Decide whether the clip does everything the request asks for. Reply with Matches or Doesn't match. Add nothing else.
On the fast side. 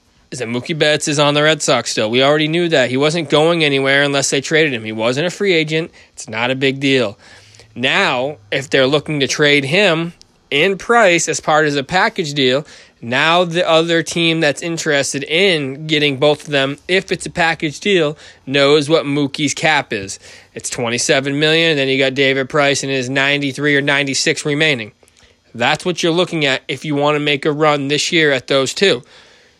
Matches